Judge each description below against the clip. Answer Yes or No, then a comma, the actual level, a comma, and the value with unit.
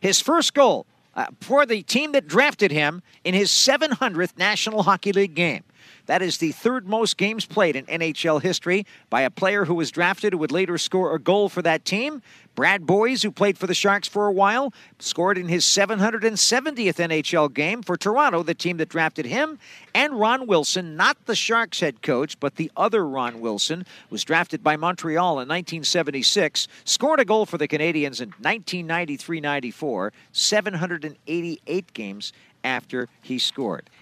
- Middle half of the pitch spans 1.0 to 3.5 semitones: No, average, 4.8 semitones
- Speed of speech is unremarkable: Yes, average, 170 wpm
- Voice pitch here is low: No, medium, 185 Hz